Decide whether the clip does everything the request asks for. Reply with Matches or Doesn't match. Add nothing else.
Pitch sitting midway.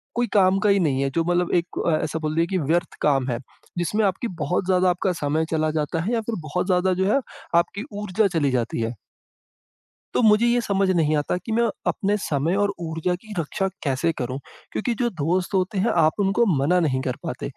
Matches